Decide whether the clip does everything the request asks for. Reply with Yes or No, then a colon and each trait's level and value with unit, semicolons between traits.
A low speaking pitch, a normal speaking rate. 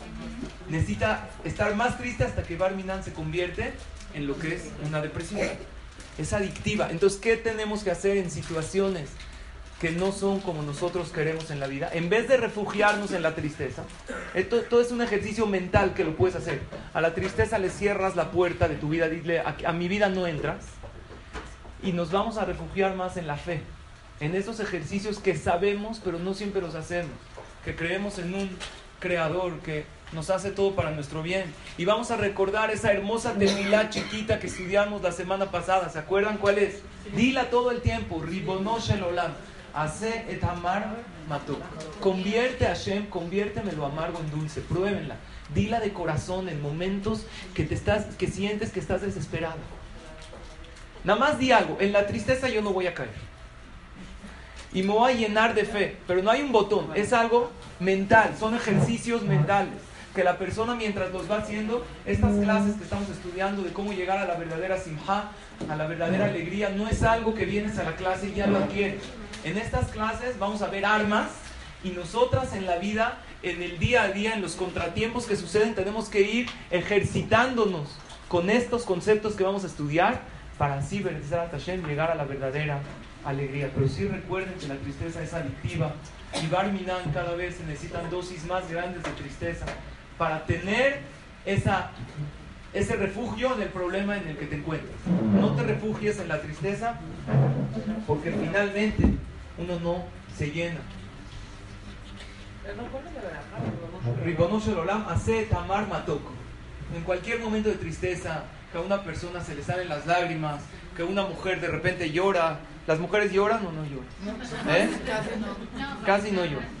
No: medium, 185 Hz; average, 170 wpm